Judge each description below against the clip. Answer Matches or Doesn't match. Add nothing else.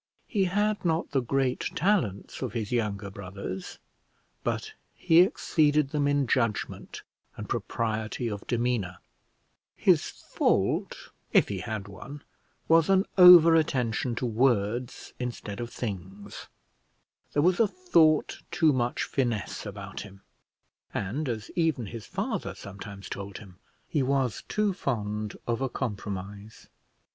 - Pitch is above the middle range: Doesn't match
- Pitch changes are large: Matches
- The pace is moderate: Doesn't match